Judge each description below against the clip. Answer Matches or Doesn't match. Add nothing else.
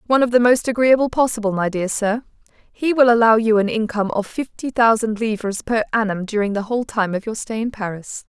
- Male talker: Doesn't match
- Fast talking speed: Matches